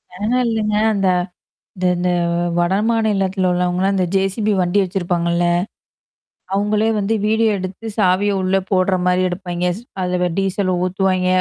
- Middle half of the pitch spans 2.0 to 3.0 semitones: Yes, narrow, 2.4 semitones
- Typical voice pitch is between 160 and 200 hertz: Yes, high, 190 Hz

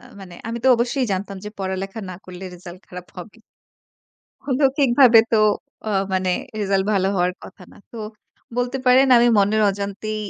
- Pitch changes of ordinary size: Yes, average, 4.1 semitones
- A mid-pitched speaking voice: No, high, 200 Hz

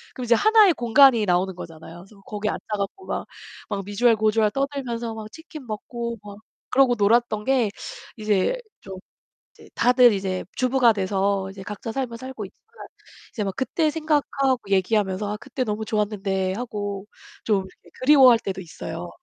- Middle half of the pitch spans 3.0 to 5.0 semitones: Yes, average, 4.3 semitones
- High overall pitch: Yes, high, 215 Hz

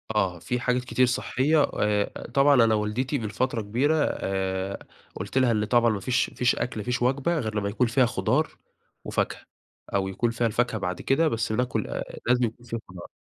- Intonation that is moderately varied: Yes, average, 3.2 semitones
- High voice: No, low, 120 Hz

